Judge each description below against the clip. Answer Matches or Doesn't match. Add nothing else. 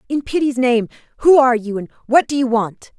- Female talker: Matches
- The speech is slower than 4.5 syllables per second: Doesn't match